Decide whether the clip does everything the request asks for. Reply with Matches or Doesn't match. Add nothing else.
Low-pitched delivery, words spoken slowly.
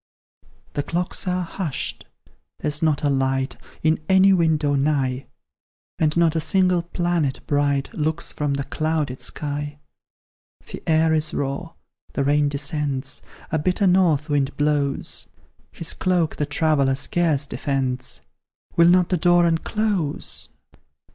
Doesn't match